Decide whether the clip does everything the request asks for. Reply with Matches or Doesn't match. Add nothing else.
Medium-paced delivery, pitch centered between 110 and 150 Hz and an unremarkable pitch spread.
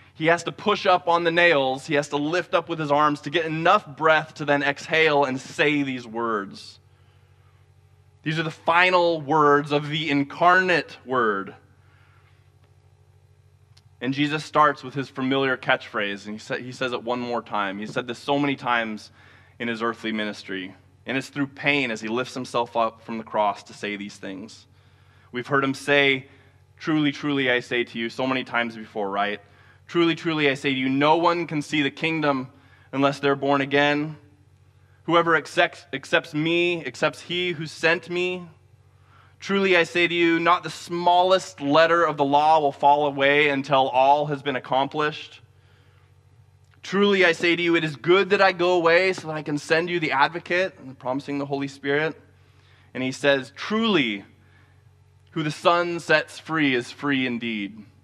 Doesn't match